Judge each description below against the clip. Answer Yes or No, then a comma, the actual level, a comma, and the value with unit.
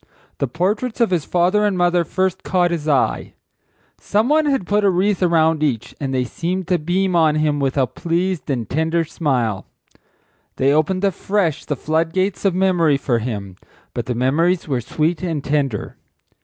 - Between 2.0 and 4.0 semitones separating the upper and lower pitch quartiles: No, average, 4.8 semitones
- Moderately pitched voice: Yes, medium, 165 Hz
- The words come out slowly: No, average, 180 wpm